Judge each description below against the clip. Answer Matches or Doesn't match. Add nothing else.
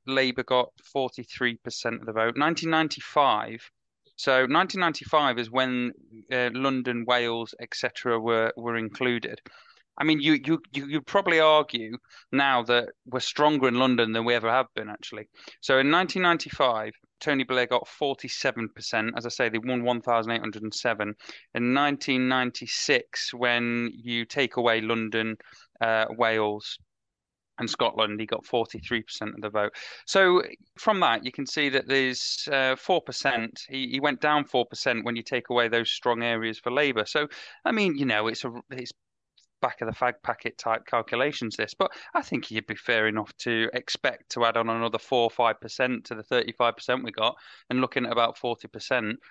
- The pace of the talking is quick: Doesn't match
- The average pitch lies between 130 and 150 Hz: Doesn't match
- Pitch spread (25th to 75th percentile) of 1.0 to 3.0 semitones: Matches